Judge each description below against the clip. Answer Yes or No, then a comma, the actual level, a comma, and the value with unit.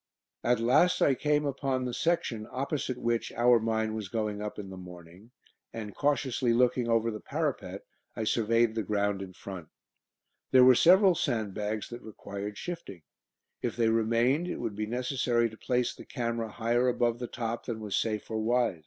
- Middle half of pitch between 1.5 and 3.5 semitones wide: Yes, average, 2.7 semitones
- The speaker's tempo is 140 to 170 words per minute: No, average, 180 wpm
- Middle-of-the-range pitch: No, low, 115 Hz